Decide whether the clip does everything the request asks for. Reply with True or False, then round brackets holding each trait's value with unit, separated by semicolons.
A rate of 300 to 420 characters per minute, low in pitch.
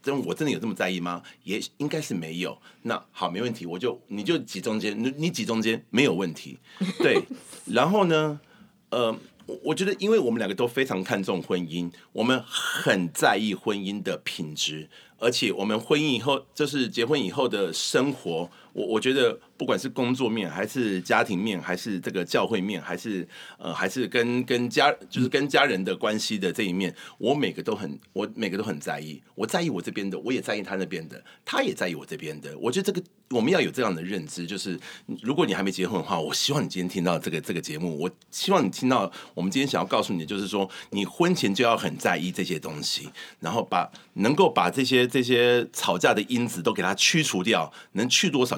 True (315 characters per minute; 120 Hz)